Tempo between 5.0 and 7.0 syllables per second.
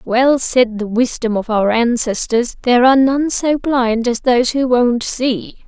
No: 4.2 syllables/s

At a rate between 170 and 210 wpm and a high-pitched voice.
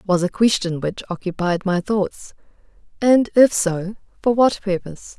No: average, 150 wpm; high, 195 Hz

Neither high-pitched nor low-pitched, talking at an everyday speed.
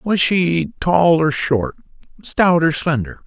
Yes: medium, 155 Hz; average, 145 wpm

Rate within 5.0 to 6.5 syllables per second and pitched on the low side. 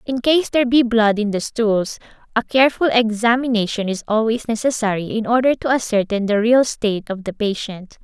No: 5.4 syllables/s; high, 225 Hz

